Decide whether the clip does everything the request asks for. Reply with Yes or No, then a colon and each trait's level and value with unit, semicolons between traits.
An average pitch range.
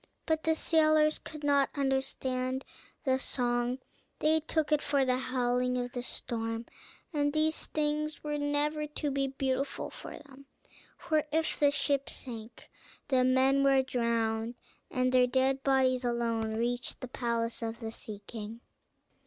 Yes: average, 3.1 semitones